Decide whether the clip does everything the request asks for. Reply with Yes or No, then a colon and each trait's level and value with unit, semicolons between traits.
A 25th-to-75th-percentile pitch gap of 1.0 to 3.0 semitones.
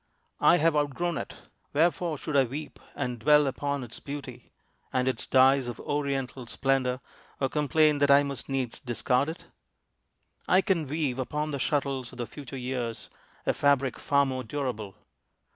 Yes: narrow, 2.5 semitones